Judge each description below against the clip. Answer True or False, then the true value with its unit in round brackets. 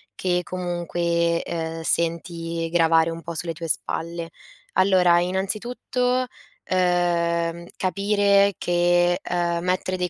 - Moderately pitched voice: True (175 Hz)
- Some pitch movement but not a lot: False (1.6 semitones)